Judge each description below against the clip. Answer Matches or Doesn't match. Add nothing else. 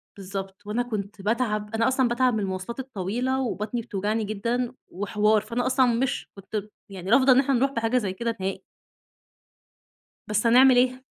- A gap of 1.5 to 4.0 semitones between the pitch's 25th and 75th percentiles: Matches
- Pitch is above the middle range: Matches